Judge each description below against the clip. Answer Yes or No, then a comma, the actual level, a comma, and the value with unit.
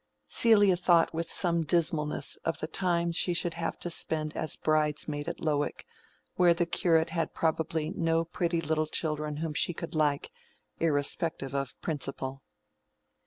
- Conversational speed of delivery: Yes, average, 150 wpm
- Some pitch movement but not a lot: No, narrow, 1.9 semitones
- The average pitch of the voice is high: No, medium, 160 Hz